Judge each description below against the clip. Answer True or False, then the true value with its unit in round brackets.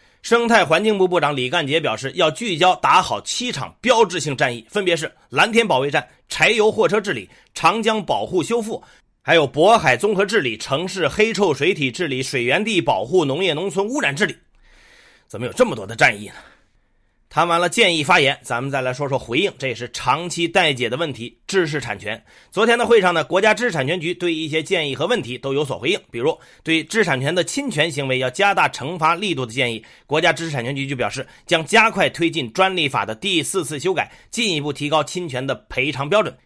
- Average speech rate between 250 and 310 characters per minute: False (325 characters per minute)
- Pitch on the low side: False (165 Hz)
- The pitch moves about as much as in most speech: False (6.9 semitones)